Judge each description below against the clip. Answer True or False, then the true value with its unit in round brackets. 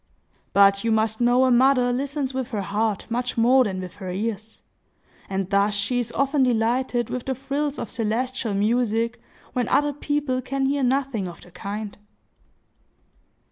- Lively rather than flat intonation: False (3.8 semitones)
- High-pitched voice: True (240 Hz)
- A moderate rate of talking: True (165 wpm)